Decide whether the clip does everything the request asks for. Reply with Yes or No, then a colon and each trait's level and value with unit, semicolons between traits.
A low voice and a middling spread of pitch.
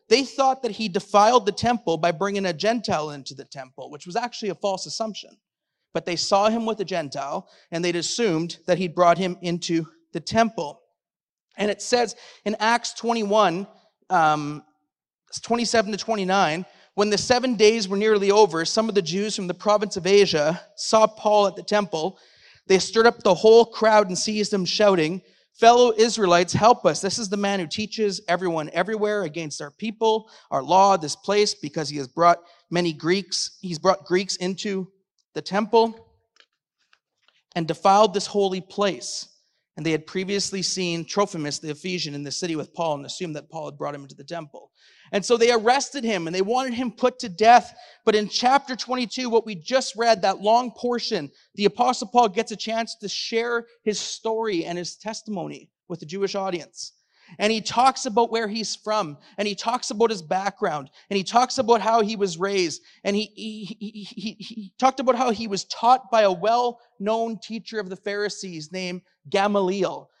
No: high, 205 Hz; average, 4.2 semitones